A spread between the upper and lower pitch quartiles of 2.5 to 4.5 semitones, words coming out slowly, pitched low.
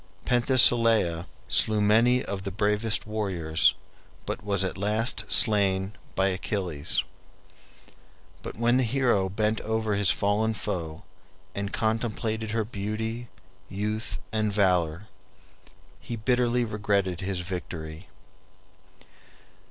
Yes: average, 2.8 semitones; slow, 105 wpm; low, 105 Hz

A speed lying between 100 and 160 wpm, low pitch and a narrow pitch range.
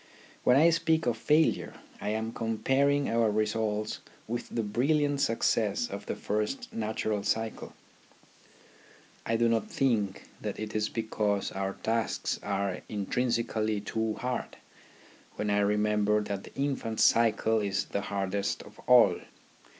Yes: average, 140 wpm; low, 110 Hz; narrow, 2.2 semitones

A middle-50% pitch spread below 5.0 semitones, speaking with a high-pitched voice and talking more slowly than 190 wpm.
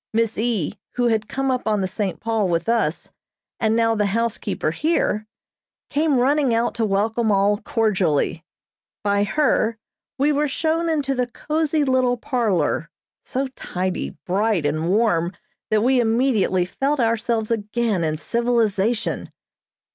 Yes: average, 3.7 semitones; high, 225 Hz; average, 140 wpm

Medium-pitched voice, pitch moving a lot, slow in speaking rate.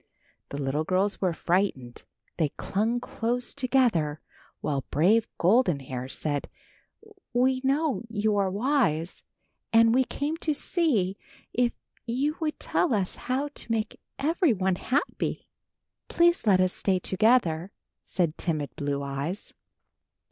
No: high, 205 Hz; wide, 7.8 semitones; slow, 125 wpm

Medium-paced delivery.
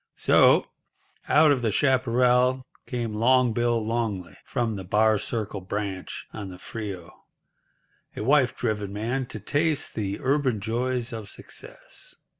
No: slow, 125 wpm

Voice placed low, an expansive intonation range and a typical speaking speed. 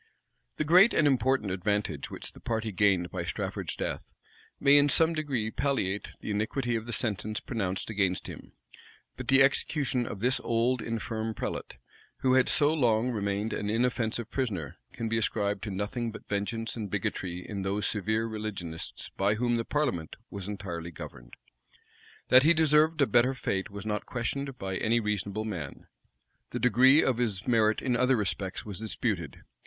No: low, 110 Hz; average, 4.0 semitones; average, 170 wpm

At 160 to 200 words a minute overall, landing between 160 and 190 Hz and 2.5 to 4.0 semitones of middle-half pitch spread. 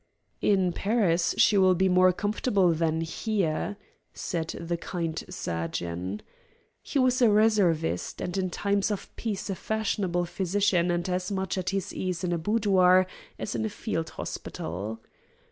No: average, 150 wpm; medium, 185 Hz; average, 3.3 semitones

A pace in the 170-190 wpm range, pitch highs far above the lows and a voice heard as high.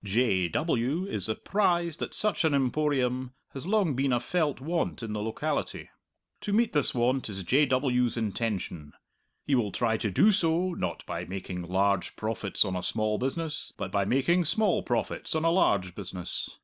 No: average, 175 wpm; wide, 7.8 semitones; low, 125 Hz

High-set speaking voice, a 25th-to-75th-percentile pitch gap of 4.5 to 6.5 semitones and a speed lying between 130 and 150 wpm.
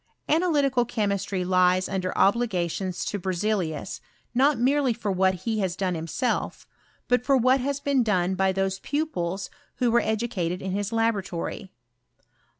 Yes: high, 205 Hz; average, 4.9 semitones; average, 145 wpm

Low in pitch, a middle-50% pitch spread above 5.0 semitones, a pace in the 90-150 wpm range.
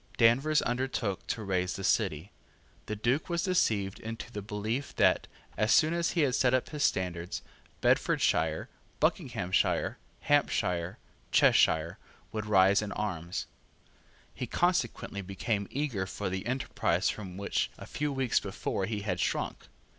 Yes: low, 105 Hz; wide, 5.4 semitones; average, 140 wpm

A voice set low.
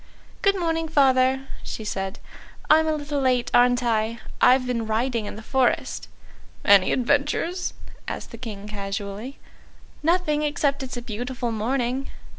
No: very high, 250 Hz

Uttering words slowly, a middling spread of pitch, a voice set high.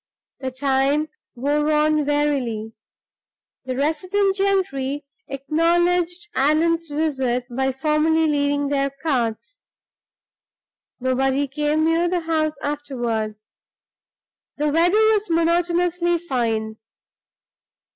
Yes: slow, 90 wpm; average, 3.8 semitones; very high, 295 Hz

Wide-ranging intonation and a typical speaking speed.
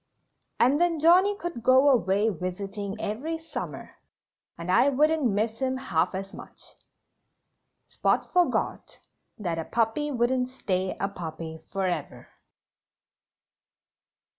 No: wide, 7.0 semitones; slow, 115 wpm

